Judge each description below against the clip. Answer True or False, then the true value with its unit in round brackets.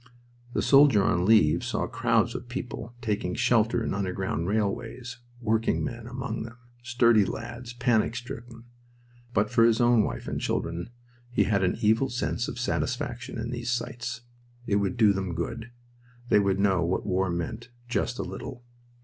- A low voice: True (115 Hz)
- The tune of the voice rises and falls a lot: False (3.4 semitones)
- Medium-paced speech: True (165 wpm)